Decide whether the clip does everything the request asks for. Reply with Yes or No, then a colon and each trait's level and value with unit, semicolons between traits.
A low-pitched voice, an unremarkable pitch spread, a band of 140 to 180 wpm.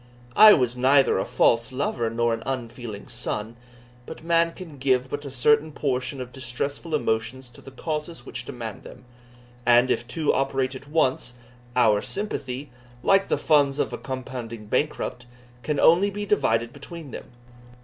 Yes: low, 130 Hz; average, 3.6 semitones; average, 160 wpm